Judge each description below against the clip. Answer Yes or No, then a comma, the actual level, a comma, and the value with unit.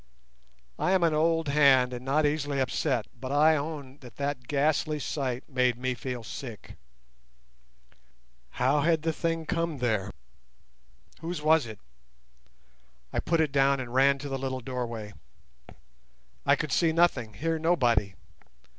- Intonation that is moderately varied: Yes, average, 3.7 semitones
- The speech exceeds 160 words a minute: No, average, 145 wpm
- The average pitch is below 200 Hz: Yes, medium, 140 Hz